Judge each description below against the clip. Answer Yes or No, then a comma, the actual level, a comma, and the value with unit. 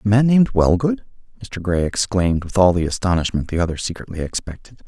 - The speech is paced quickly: No, average, 185 wpm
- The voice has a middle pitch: No, very low, 95 Hz